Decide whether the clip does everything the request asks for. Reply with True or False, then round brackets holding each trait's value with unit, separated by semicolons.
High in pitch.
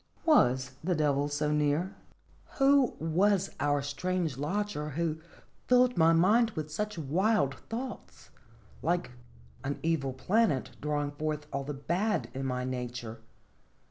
False (155 Hz)